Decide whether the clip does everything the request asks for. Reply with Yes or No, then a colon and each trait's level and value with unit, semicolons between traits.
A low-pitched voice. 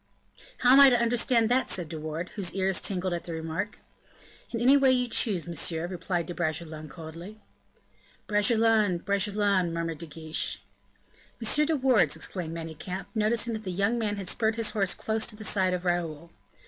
No: high, 190 Hz